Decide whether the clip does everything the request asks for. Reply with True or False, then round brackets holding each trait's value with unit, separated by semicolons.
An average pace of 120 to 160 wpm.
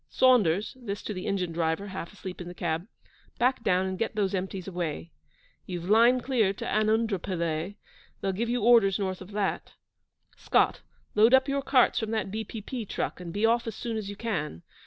False (190 wpm)